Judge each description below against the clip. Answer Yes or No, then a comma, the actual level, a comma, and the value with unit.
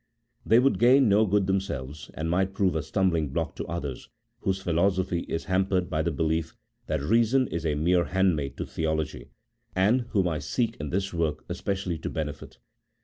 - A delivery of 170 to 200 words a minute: Yes, average, 180 wpm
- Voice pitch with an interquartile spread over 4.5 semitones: No, average, 3.8 semitones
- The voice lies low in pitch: Yes, very low, 90 Hz